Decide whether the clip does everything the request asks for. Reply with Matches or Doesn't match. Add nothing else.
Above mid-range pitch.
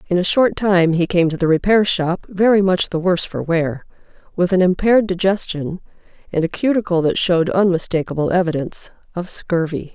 Doesn't match